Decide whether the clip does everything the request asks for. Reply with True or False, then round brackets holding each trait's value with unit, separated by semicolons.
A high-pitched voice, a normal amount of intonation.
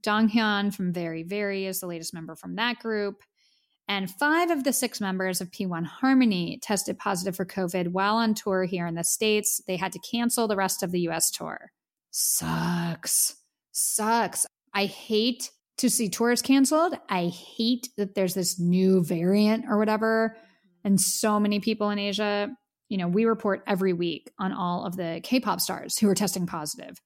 True (200 Hz; 3.3 semitones)